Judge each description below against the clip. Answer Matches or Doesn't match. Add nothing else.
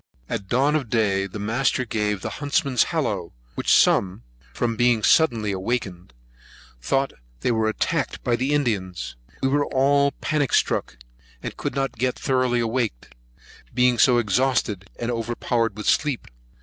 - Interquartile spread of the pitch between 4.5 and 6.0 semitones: Doesn't match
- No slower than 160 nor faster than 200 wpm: Doesn't match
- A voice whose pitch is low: Matches